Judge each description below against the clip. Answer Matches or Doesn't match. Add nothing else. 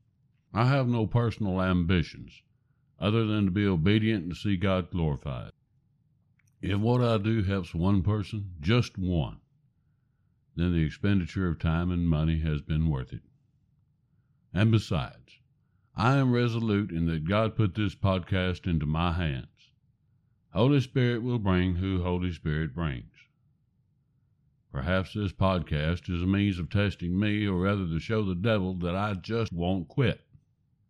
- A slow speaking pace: Doesn't match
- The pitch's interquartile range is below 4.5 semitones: Doesn't match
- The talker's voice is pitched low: Matches